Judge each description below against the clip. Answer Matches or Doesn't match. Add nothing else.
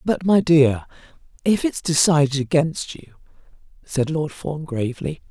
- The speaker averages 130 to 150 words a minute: Matches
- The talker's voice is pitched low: Doesn't match